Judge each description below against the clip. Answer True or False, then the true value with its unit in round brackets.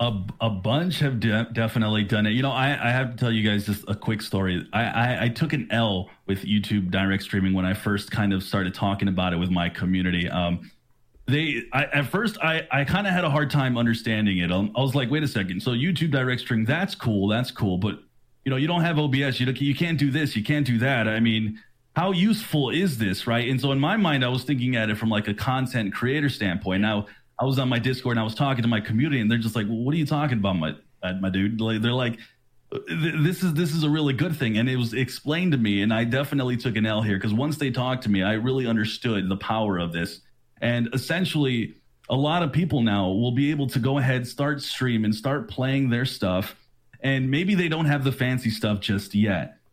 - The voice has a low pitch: True (120 Hz)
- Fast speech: True (245 wpm)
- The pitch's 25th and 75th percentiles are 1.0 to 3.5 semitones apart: False (4.8 semitones)